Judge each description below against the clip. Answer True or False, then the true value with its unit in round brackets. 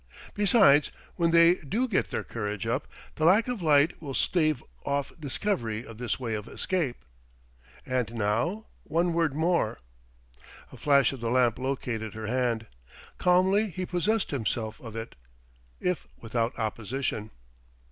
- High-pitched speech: False (140 Hz)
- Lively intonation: True (7.2 semitones)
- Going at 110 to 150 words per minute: True (145 wpm)